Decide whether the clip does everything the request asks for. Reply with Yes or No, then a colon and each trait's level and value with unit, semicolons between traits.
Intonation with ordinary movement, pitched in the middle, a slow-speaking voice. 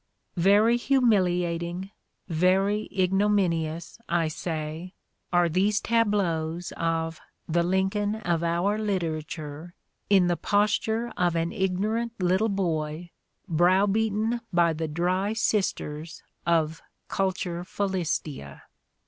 Yes: average, 3.5 semitones; medium, 180 Hz; slow, 105 wpm